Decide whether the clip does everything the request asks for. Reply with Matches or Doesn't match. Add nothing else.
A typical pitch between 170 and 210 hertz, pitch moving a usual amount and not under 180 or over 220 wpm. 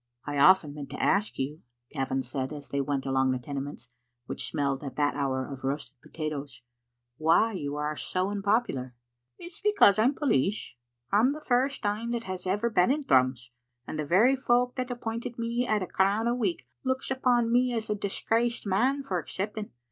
Doesn't match